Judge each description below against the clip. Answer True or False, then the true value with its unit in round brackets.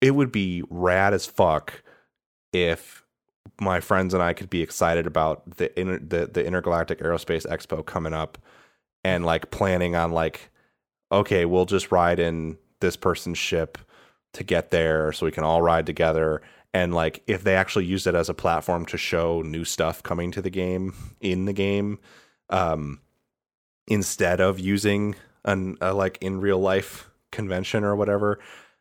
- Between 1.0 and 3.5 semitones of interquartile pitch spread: True (2.8 semitones)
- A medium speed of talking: True (165 wpm)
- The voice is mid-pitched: False (90 Hz)